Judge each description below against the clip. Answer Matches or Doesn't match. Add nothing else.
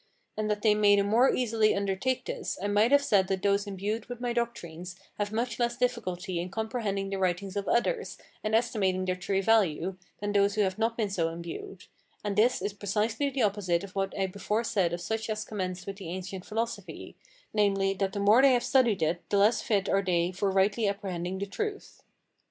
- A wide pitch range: Doesn't match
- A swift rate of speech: Matches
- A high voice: Matches